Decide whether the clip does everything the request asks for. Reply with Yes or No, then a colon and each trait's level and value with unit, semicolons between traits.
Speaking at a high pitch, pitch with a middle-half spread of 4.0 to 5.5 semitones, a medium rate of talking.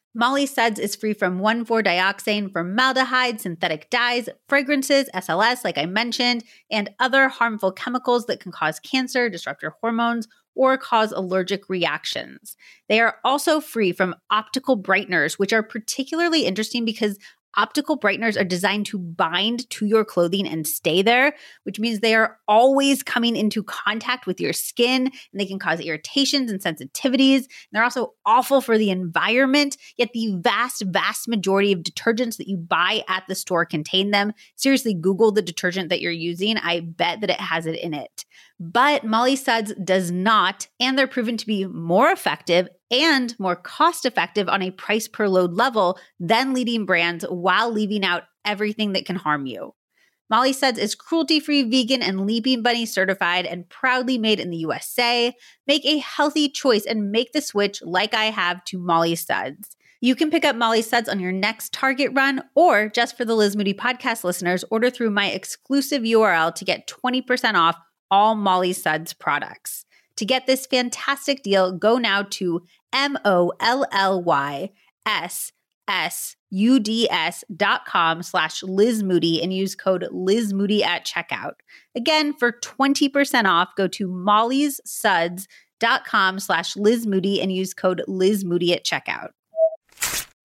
Yes: high, 215 Hz; average, 5.1 semitones; average, 160 wpm